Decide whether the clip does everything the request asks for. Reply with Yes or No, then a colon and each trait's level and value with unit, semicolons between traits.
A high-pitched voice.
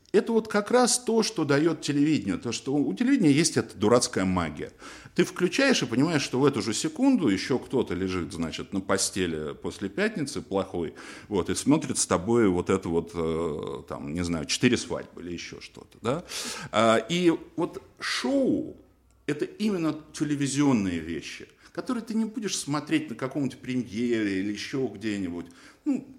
No: low, 135 Hz